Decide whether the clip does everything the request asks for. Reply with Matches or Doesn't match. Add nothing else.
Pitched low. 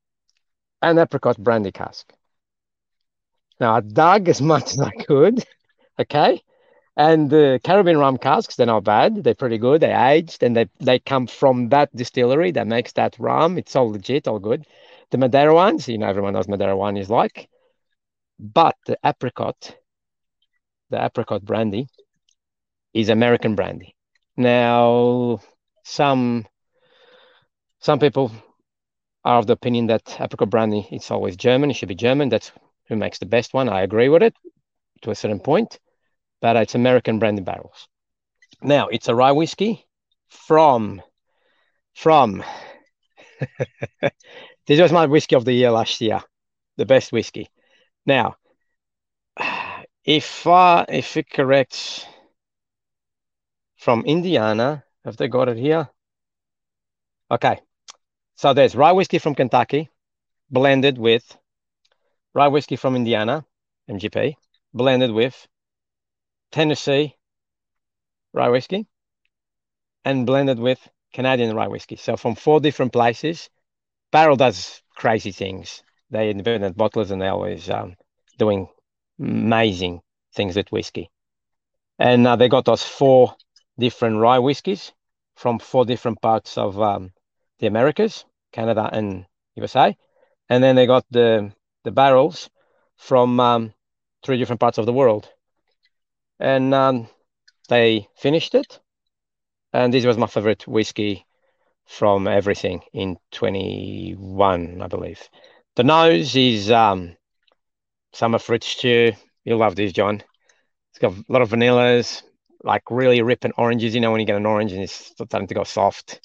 Matches